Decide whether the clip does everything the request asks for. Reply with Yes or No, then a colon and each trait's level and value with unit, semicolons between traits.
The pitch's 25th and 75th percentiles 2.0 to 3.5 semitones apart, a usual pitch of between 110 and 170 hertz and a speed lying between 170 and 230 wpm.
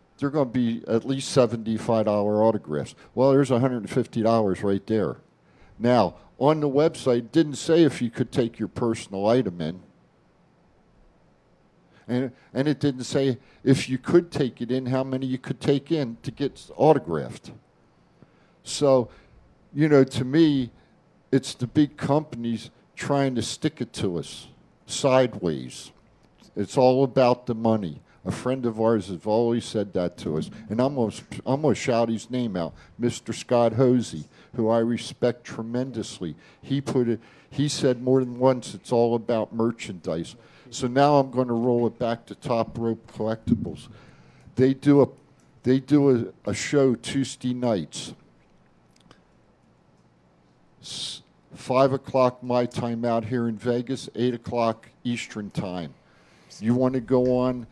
No: average, 2.9 semitones; low, 125 Hz; average, 155 wpm